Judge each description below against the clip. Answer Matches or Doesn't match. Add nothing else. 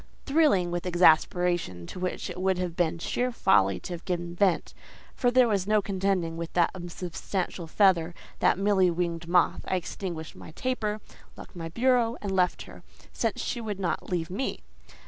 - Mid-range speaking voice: Matches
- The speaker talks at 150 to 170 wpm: Matches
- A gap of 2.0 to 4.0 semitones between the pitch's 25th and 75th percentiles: Matches